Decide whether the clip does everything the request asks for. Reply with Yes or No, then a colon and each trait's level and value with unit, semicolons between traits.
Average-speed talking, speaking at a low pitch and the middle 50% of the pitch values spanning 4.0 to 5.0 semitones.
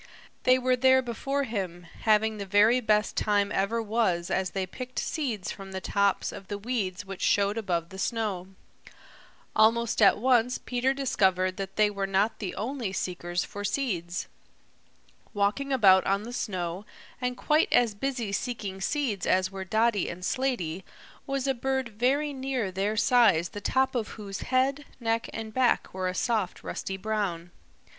No: average, 165 wpm; high, 215 Hz; average, 4.5 semitones